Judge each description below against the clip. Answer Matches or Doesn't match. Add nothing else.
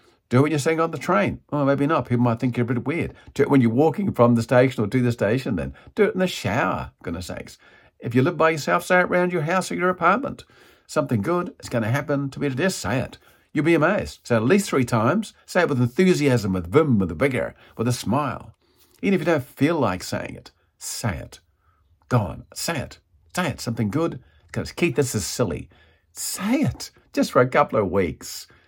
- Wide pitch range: Matches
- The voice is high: Doesn't match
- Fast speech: Matches